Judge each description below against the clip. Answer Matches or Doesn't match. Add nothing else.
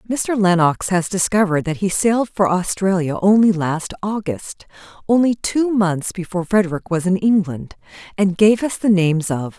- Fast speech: Doesn't match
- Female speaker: Matches